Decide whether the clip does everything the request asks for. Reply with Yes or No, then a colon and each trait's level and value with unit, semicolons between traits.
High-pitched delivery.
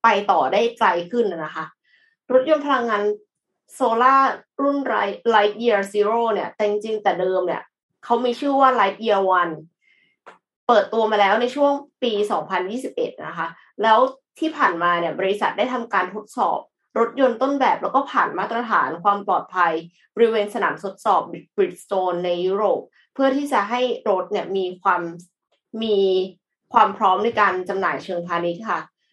Yes: high, 210 Hz